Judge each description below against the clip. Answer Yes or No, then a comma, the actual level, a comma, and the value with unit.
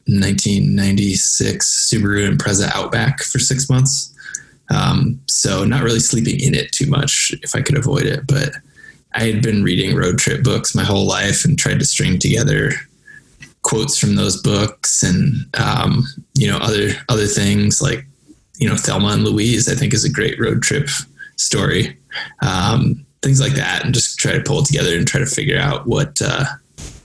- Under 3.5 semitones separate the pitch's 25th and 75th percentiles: No, average, 4.2 semitones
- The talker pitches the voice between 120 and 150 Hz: Yes, low, 135 Hz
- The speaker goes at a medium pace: Yes, average, 175 wpm